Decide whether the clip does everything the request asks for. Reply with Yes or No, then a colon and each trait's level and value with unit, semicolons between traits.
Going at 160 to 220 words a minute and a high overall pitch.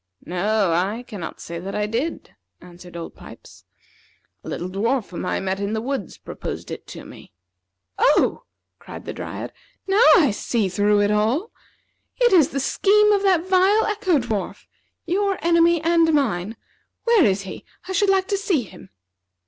Yes: average, 170 wpm; very high, 250 Hz